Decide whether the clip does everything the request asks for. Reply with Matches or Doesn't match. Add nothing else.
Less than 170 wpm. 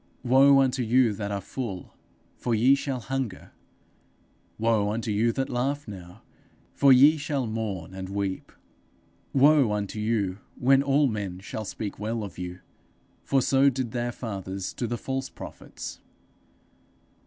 Matches